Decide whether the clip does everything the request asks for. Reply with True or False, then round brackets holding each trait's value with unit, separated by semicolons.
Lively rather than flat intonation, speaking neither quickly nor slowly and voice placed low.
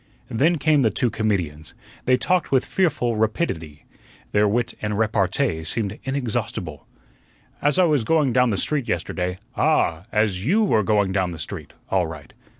True (6.5 semitones; 165 wpm; 110 Hz)